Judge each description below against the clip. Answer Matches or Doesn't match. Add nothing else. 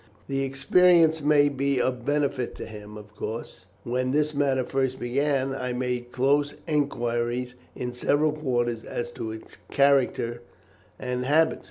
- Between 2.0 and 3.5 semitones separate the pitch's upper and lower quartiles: Matches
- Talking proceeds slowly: Doesn't match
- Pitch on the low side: Matches